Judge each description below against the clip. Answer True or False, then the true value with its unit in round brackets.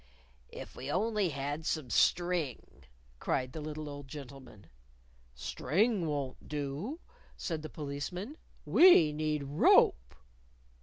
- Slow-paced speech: True (110 wpm)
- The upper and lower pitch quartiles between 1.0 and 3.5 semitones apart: False (4.0 semitones)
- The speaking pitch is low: False (150 Hz)